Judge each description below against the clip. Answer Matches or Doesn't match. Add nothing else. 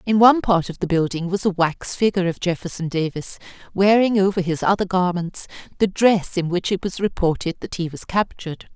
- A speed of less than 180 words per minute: Doesn't match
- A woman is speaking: Matches